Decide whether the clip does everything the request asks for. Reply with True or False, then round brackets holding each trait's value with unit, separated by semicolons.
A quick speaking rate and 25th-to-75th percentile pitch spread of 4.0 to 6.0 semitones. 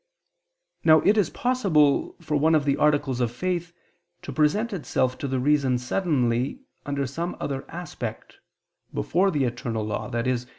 False (155 wpm; 5.0 semitones)